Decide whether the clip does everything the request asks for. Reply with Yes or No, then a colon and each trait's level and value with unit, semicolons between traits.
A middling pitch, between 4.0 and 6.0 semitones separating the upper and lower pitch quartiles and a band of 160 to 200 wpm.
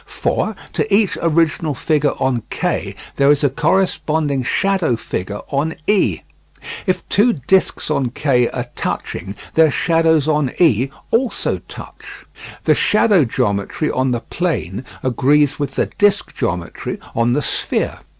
No: medium, 145 Hz; average, 5.0 semitones; average, 140 wpm